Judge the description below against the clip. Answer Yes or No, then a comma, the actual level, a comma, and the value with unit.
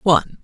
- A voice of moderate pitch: Yes, medium, 170 Hz